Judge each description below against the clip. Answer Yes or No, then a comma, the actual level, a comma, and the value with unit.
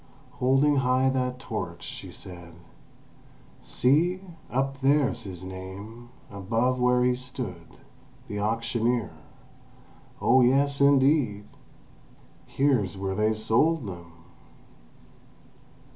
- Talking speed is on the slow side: Yes, slow, 95 wpm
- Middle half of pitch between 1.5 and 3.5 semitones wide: No, average, 4.8 semitones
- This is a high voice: No, low, 125 Hz